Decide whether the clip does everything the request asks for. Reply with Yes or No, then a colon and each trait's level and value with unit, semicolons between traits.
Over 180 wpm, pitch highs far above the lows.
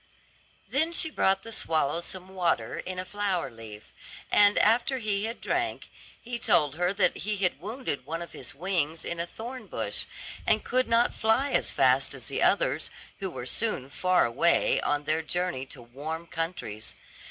No: average, 175 wpm; wide, 6.0 semitones